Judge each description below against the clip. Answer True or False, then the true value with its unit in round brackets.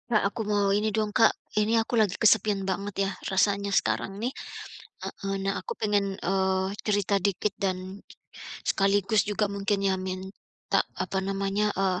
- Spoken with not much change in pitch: True (1.4 semitones)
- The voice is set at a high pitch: True (200 Hz)